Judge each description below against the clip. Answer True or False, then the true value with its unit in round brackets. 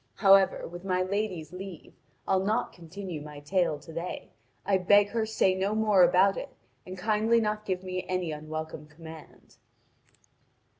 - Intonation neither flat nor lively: True (3.3 semitones)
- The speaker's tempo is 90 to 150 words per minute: False (165 wpm)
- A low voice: False (185 Hz)